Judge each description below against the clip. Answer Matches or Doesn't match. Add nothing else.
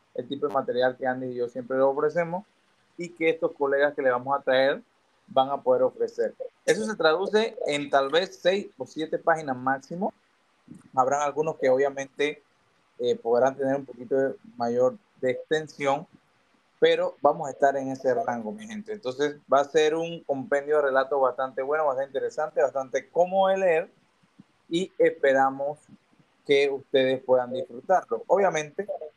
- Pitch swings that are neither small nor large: Doesn't match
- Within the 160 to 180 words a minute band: Matches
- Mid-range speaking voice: Matches